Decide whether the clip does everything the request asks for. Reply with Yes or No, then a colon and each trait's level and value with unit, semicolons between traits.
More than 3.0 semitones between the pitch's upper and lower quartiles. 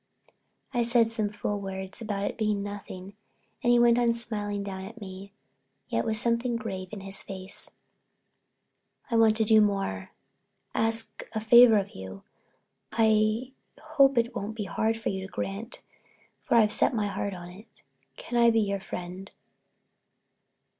No: average, 2.7 semitones